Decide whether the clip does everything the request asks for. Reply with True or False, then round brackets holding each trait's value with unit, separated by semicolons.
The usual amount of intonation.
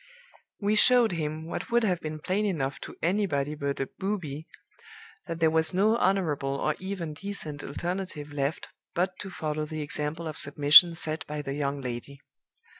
True (4.3 semitones)